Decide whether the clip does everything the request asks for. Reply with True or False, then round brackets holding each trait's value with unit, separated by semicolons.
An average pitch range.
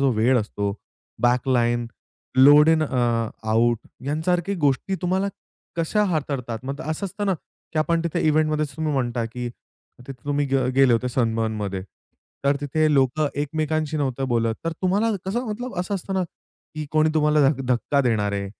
True (4.6 semitones)